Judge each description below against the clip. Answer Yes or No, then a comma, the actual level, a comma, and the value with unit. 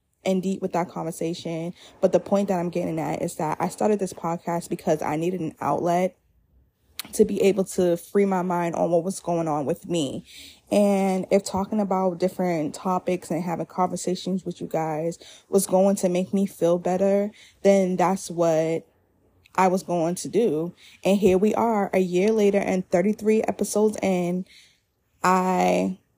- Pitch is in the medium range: Yes, medium, 180 Hz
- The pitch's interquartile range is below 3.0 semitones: Yes, narrow, 2.4 semitones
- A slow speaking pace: No, average, 175 wpm